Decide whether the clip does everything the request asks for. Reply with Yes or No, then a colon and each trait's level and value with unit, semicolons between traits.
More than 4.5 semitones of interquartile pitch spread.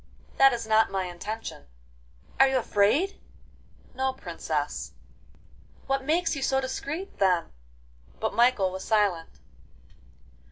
Yes: average, 5.1 semitones